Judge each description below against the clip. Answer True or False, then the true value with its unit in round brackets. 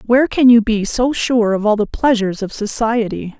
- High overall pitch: True (225 Hz)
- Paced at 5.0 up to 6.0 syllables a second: True (5.2 syllables/s)